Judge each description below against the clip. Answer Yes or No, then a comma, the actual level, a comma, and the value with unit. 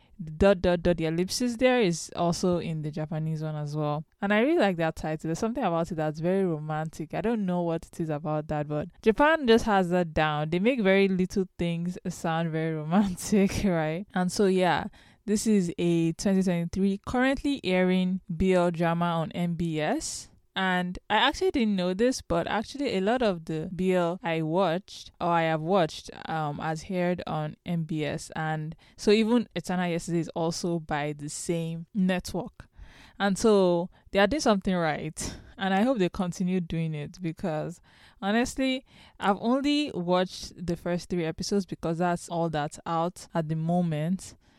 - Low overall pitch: No, medium, 175 Hz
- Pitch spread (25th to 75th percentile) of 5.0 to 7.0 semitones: No, average, 3.3 semitones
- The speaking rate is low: No, average, 175 wpm